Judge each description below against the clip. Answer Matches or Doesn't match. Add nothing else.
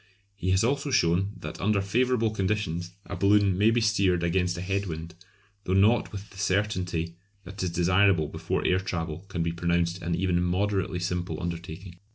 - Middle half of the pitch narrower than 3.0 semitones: Matches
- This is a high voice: Doesn't match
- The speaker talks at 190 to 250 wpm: Doesn't match